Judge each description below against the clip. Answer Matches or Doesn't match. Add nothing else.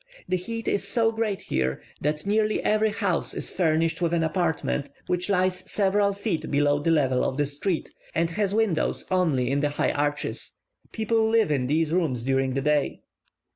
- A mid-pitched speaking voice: Matches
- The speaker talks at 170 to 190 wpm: Matches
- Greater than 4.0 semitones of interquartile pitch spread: Matches